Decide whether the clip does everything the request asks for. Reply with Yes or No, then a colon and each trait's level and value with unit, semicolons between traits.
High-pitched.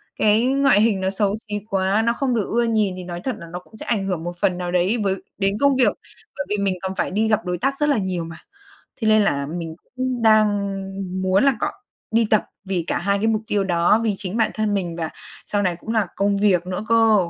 Yes: high, 205 Hz